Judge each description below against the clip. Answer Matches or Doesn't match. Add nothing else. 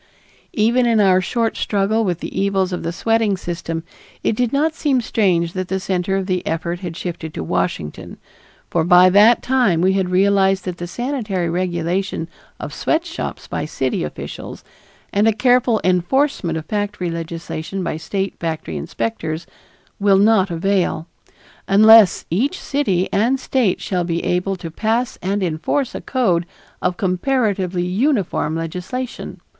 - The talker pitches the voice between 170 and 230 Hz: Matches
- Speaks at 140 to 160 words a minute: Matches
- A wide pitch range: Doesn't match